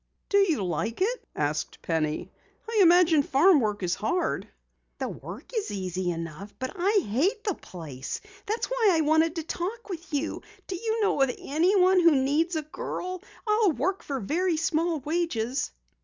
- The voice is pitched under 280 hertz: No, very high, 320 Hz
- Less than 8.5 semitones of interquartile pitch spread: No, wide, 9.0 semitones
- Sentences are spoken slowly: No, average, 170 wpm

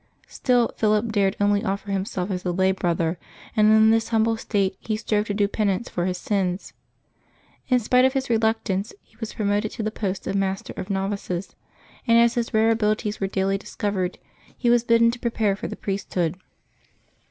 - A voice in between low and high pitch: No, high, 210 Hz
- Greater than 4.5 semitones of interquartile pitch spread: No, average, 2.7 semitones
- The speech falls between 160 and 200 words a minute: Yes, average, 185 wpm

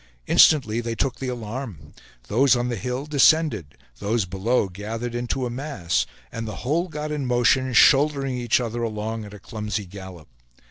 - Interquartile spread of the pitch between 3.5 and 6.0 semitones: Yes, average, 3.9 semitones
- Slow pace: No, average, 170 wpm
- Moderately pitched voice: No, low, 120 Hz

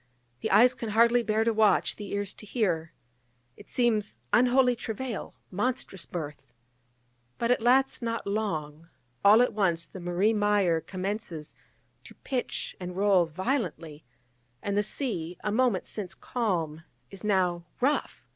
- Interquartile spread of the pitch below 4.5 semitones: No, average, 4.8 semitones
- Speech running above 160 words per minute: No, average, 145 wpm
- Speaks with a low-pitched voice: No, high, 205 Hz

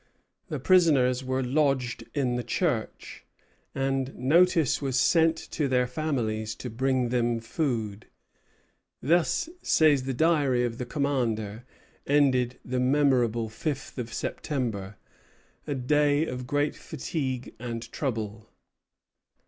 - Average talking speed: No, slow, 115 wpm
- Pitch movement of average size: Yes, average, 3.3 semitones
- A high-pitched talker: No, low, 130 Hz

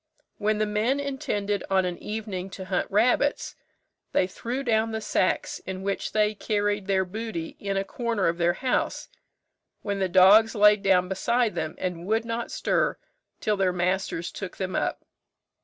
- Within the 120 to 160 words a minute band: No, average, 170 wpm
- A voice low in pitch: No, high, 205 Hz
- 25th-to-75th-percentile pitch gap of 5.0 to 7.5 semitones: No, average, 3.0 semitones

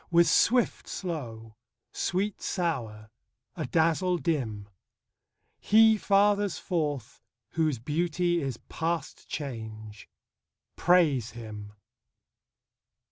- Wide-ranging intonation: Yes, wide, 7.8 semitones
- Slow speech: Yes, slow, 80 wpm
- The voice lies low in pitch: No, medium, 160 Hz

